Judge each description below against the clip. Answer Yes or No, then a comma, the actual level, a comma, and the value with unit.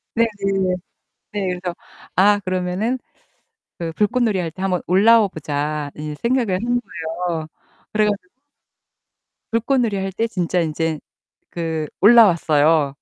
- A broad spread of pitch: No, average, 4.7 semitones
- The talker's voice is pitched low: No, medium, 185 Hz